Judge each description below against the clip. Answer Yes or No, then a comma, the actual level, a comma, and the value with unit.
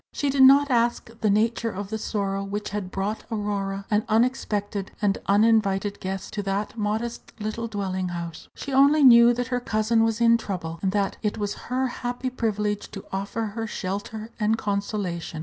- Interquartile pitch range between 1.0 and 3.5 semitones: Yes, average, 2.7 semitones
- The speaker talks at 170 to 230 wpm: Yes, average, 180 wpm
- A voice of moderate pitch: No, high, 210 Hz